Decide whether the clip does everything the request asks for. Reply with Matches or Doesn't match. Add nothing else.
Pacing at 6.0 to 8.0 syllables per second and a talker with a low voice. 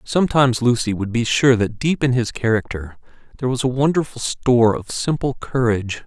Doesn't match